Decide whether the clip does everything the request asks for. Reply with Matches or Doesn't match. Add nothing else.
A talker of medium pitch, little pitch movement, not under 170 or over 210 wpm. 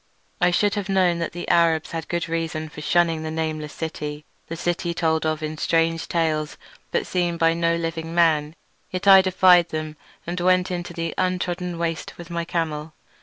Matches